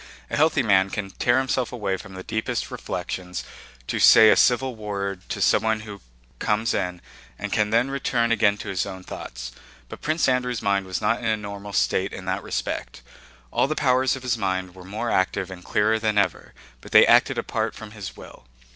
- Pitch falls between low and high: No, low, 105 Hz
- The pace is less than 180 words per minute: No, average, 200 wpm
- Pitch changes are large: No, average, 3.5 semitones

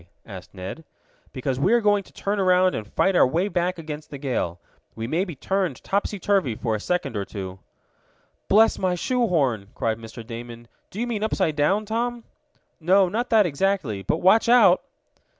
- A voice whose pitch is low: No, medium, 175 Hz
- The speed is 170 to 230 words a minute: Yes, average, 185 wpm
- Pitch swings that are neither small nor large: No, wide, 9.0 semitones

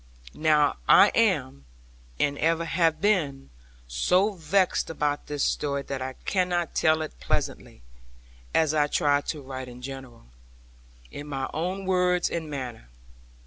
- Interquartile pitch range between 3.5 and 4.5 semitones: Yes, average, 3.8 semitones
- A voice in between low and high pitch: Yes, medium, 150 Hz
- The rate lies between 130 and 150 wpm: Yes, average, 140 wpm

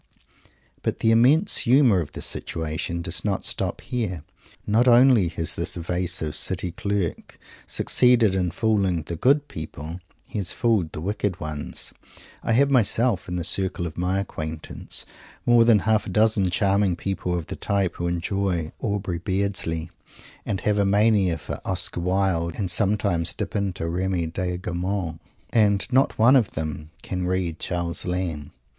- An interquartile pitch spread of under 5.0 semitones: Yes, average, 3.7 semitones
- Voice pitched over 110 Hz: No, very low, 95 Hz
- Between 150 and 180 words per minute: Yes, average, 160 wpm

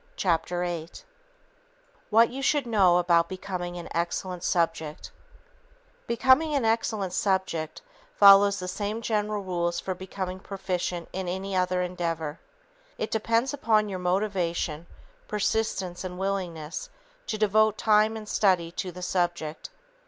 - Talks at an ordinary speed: No, slow, 130 wpm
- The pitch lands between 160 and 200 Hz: Yes, medium, 185 Hz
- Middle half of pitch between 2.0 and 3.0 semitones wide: No, average, 3.4 semitones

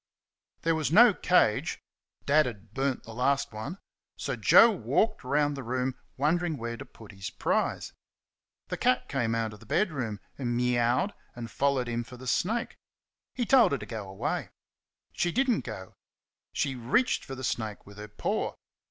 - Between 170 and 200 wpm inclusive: Yes, average, 175 wpm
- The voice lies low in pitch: Yes, low, 130 Hz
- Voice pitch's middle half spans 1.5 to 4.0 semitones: No, wide, 5.6 semitones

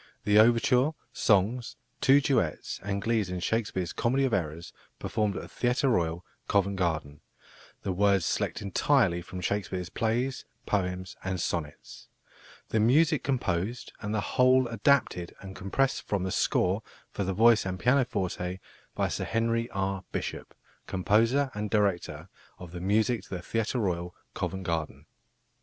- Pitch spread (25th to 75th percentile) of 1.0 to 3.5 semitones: No, average, 4.4 semitones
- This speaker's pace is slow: No, average, 150 wpm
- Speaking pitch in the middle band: No, low, 100 Hz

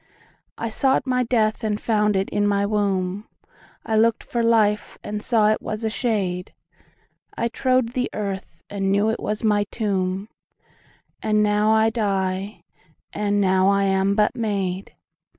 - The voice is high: Yes, high, 210 Hz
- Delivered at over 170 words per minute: No, average, 145 wpm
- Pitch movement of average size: No, narrow, 2.0 semitones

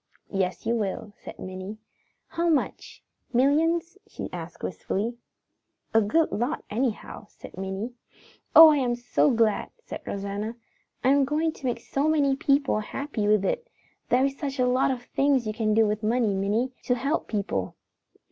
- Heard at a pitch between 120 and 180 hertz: No, high, 240 Hz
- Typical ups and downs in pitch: Yes, average, 4.8 semitones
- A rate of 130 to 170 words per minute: Yes, average, 160 wpm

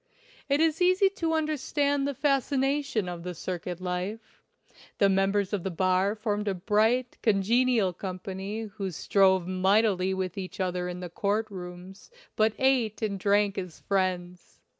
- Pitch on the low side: No, high, 200 Hz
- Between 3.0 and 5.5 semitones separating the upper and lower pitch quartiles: Yes, average, 4.0 semitones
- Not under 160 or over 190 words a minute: No, average, 150 wpm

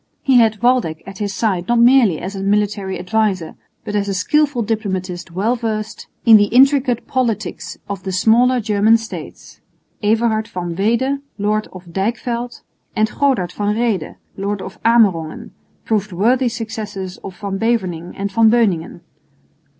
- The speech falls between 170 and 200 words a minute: No, average, 150 wpm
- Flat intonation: No, average, 3.4 semitones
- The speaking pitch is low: No, high, 210 Hz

